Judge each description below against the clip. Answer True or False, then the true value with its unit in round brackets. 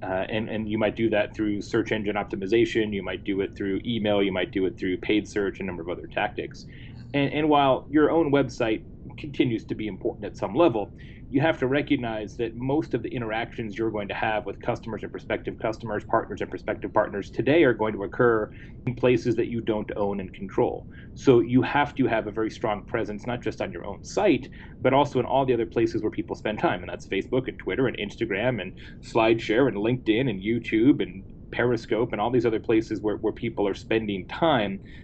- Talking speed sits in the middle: False (225 wpm)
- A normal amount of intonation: True (3.0 semitones)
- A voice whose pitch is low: True (115 Hz)